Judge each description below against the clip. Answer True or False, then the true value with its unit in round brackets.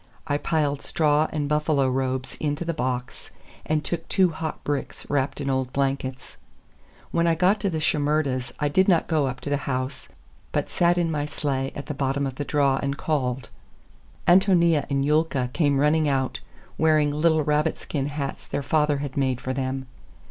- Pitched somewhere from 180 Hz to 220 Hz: False (145 Hz)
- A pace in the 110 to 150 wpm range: False (185 wpm)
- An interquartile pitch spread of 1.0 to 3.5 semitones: True (2.6 semitones)